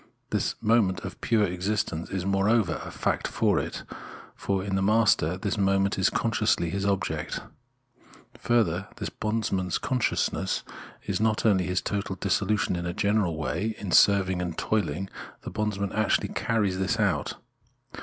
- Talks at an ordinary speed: Yes, average, 155 wpm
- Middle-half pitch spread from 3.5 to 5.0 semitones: No, average, 2.7 semitones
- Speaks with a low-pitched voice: Yes, low, 100 Hz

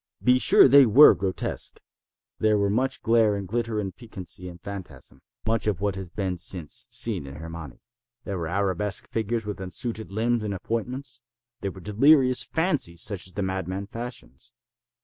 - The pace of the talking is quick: No, average, 165 wpm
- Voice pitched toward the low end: Yes, low, 100 Hz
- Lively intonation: No, average, 3.9 semitones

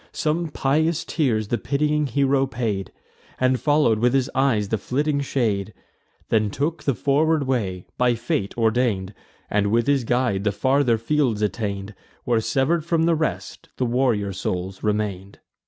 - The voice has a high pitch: No, low, 125 Hz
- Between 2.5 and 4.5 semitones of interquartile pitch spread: No, average, 5.0 semitones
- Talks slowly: No, average, 155 wpm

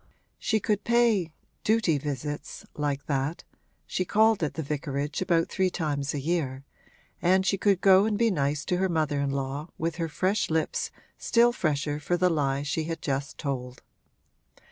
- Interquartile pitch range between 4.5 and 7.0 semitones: Yes, average, 4.9 semitones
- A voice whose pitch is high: No, medium, 160 Hz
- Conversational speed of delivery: Yes, average, 170 wpm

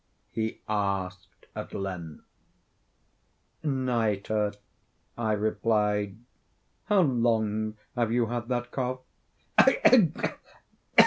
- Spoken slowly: Yes, slow, 80 wpm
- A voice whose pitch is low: Yes, low, 110 Hz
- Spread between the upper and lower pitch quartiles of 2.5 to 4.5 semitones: Yes, average, 2.9 semitones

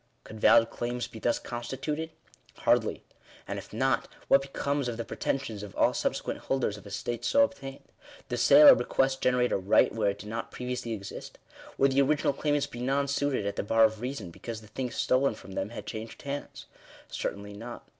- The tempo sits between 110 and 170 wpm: No, average, 195 wpm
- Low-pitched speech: Yes, low, 120 Hz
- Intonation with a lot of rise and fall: No, average, 4.0 semitones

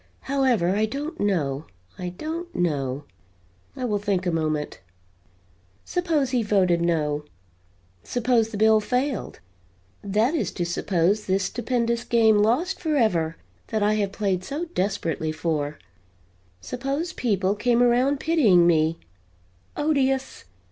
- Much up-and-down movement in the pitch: Yes, wide, 6.7 semitones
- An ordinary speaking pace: No, slow, 125 wpm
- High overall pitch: Yes, high, 210 Hz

